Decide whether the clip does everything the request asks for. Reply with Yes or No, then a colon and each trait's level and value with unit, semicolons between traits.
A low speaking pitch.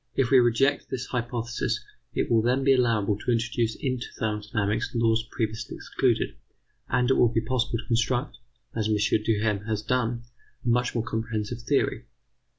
Yes: low, 115 Hz